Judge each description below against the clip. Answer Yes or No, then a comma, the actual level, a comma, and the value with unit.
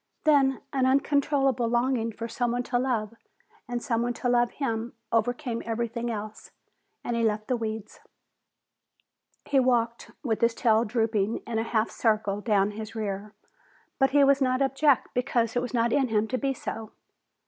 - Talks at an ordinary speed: Yes, average, 165 wpm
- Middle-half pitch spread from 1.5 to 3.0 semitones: Yes, narrow, 2.5 semitones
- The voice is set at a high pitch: Yes, high, 235 Hz